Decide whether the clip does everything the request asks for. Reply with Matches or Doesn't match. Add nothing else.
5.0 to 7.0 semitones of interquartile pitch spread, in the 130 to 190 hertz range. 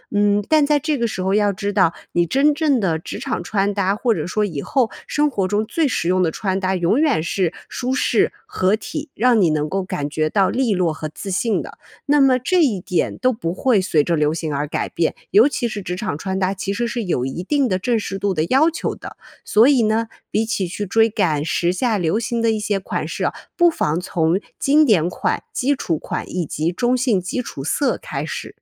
Doesn't match